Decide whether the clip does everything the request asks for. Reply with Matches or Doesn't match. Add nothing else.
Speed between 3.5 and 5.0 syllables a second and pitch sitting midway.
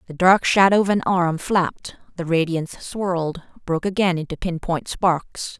Matches